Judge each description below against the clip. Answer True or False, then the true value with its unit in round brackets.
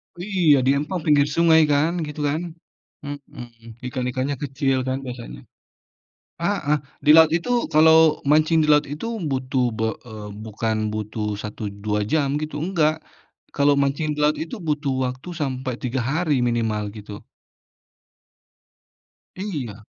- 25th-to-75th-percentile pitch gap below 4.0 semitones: False (4.3 semitones)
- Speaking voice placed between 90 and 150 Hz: True (140 Hz)